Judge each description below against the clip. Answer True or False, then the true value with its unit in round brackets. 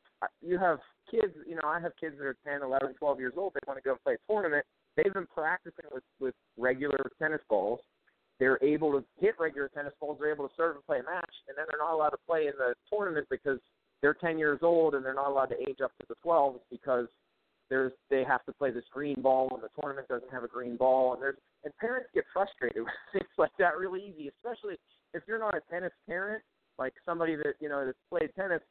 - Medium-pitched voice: True (145 Hz)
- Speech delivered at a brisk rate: True (240 wpm)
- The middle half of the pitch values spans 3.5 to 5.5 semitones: True (4.5 semitones)